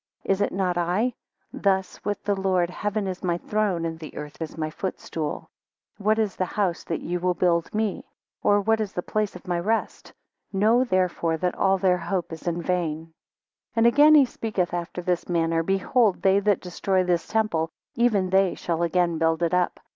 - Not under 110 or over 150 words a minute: No, average, 190 wpm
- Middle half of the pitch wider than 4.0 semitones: No, average, 3.2 semitones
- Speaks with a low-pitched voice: No, medium, 185 Hz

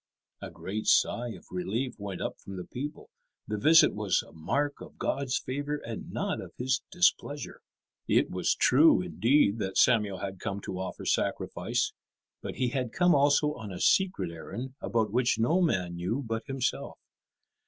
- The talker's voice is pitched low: Yes, low, 120 Hz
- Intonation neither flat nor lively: No, wide, 6.3 semitones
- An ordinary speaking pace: Yes, average, 170 wpm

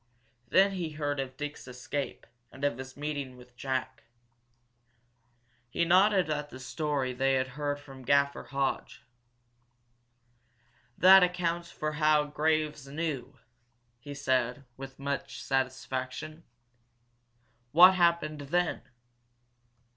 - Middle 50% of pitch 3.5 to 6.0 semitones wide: No, average, 2.9 semitones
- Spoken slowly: Yes, slow, 110 wpm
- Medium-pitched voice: Yes, medium, 145 Hz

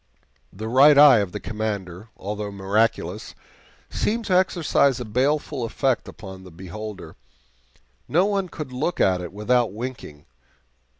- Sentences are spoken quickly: No, slow, 135 wpm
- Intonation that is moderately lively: No, wide, 6.5 semitones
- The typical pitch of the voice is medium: No, low, 110 Hz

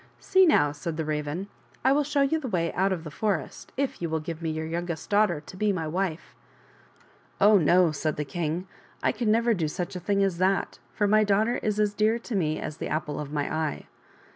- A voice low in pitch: No, medium, 180 Hz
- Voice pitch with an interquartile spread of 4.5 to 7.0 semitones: Yes, average, 5.2 semitones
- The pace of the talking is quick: Yes, fast, 245 wpm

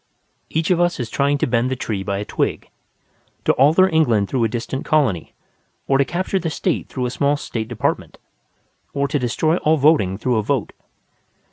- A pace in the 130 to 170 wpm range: No, average, 195 wpm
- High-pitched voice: No, low, 135 Hz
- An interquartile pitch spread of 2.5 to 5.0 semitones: No, wide, 5.4 semitones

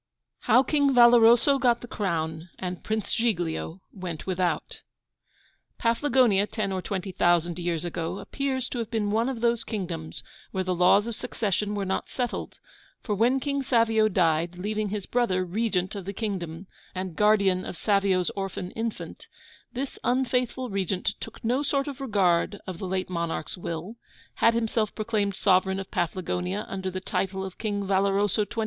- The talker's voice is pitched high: Yes, high, 200 Hz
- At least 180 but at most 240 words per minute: No, average, 165 wpm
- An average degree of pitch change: Yes, average, 4.0 semitones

